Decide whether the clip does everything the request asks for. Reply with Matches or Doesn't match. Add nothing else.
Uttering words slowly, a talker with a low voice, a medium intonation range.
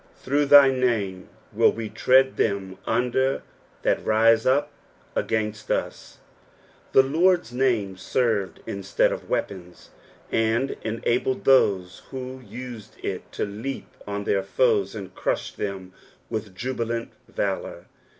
Matches